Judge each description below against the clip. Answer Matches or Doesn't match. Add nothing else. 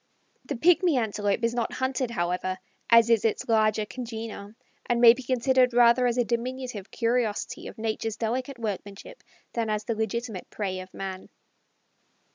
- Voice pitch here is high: Matches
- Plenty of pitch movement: Doesn't match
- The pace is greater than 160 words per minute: Doesn't match